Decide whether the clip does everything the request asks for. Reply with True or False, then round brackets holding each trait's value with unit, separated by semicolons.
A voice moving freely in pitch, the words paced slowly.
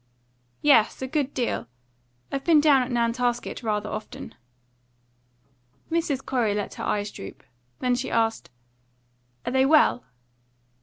False (3.6 semitones; 125 wpm)